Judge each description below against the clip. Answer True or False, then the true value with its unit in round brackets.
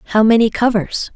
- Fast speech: False (155 wpm)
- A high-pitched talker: True (220 Hz)